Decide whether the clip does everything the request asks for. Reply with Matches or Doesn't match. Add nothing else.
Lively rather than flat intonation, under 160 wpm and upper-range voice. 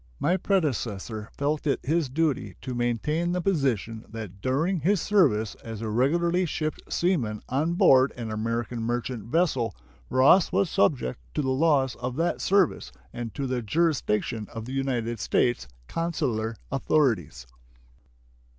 Doesn't match